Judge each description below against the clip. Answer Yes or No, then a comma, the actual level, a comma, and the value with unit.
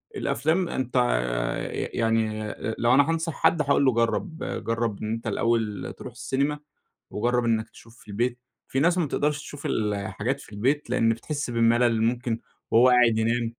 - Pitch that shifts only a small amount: No, average, 3.5 semitones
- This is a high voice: No, low, 120 Hz